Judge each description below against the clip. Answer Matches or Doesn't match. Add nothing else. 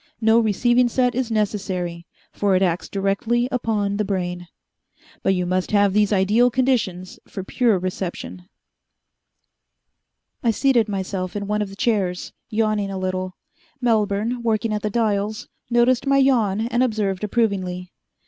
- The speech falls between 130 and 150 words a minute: Matches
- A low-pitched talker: Doesn't match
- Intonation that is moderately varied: Matches